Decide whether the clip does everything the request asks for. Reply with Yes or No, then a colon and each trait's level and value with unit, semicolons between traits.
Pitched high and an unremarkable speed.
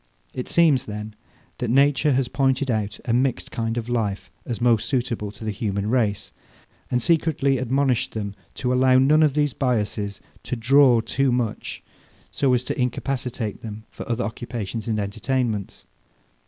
No: low, 120 Hz; average, 160 wpm